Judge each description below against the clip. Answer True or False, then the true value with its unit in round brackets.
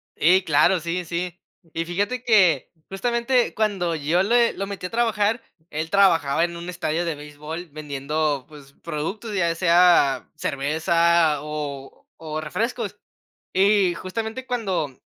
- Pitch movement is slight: False (4.7 semitones)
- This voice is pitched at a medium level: True (170 Hz)